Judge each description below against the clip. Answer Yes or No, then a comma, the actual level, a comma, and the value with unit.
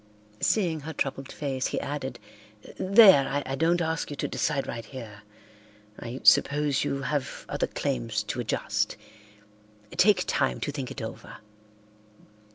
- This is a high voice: No, medium, 140 Hz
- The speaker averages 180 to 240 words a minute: No, average, 140 wpm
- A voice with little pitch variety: No, average, 3.2 semitones